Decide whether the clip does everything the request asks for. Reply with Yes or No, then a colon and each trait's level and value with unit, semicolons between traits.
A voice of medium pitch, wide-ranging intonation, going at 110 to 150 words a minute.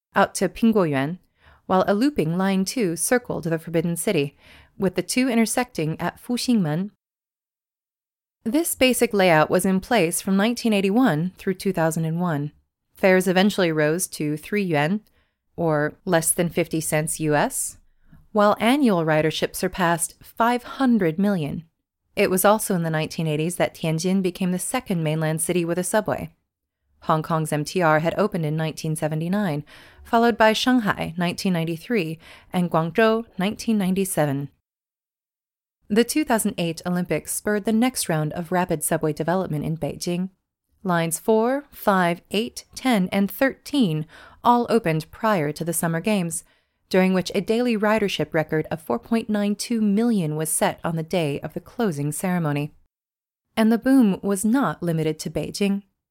No: medium, 180 Hz; average, 5.0 semitones; average, 145 wpm